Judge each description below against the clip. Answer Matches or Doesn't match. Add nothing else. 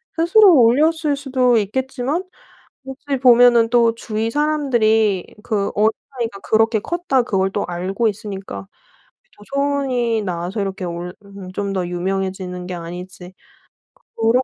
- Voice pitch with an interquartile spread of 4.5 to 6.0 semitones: Matches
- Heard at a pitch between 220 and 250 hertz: Matches